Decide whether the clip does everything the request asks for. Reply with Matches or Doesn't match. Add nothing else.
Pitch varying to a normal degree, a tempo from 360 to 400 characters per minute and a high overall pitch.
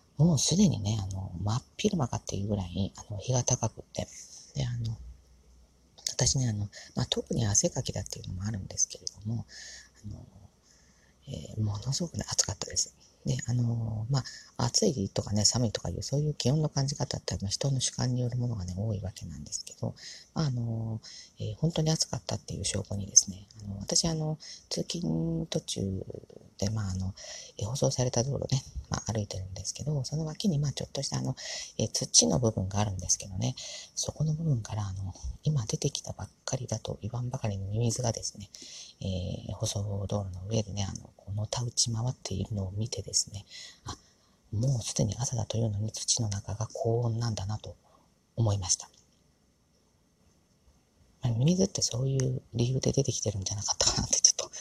Doesn't match